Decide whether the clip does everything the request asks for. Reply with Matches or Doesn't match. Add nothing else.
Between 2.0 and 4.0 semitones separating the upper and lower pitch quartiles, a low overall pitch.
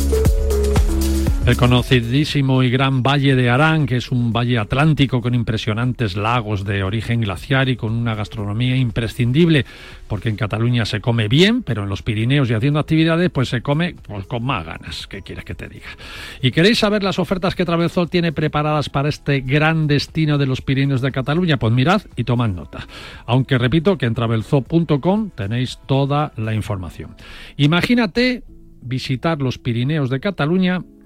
Doesn't match